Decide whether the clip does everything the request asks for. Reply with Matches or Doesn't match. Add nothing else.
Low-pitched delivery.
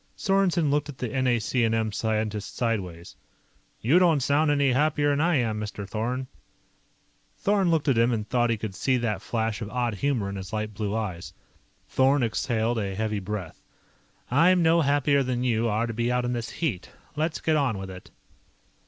Matches